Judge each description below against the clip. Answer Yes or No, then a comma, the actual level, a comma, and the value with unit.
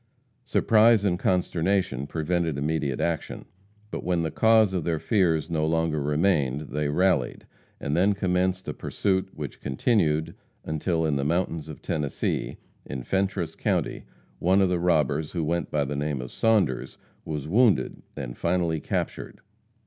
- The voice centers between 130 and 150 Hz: No, very low, 80 Hz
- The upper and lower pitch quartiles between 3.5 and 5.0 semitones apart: Yes, average, 3.9 semitones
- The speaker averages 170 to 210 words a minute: No, average, 150 wpm